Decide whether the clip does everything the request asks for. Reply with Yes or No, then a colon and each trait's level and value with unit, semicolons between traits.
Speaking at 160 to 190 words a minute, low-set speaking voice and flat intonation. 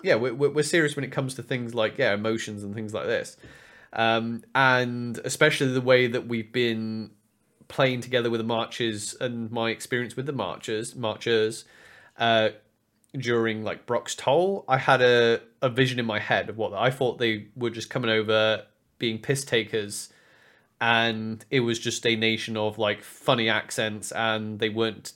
Yes: average, 180 wpm; low, 115 Hz; narrow, 2.3 semitones